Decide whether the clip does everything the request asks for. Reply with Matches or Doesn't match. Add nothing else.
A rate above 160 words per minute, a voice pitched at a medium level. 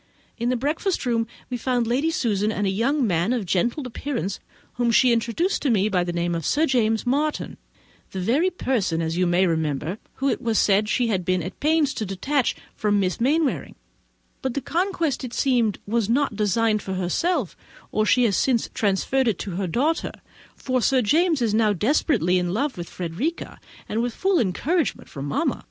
Doesn't match